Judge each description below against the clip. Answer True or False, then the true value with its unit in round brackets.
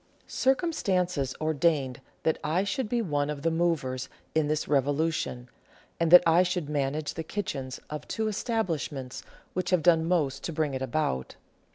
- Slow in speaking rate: False (160 wpm)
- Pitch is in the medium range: True (160 Hz)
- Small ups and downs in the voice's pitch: False (4.0 semitones)